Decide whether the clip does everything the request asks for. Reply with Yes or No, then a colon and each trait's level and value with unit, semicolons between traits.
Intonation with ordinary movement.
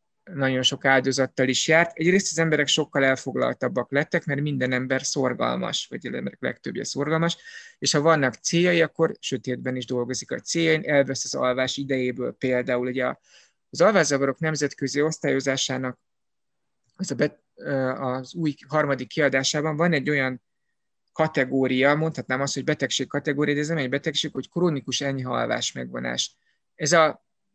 Yes: average, 3.1 semitones